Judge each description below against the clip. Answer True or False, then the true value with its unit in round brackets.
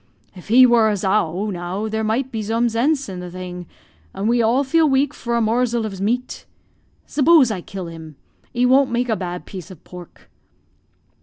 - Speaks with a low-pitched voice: False (220 Hz)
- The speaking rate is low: False (190 wpm)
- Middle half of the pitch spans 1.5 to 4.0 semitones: False (5.1 semitones)